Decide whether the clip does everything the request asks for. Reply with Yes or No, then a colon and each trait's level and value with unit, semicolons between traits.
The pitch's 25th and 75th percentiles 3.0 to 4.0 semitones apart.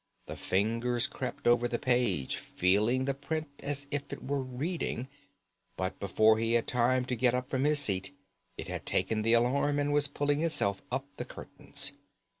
Yes: average, 3.7 semitones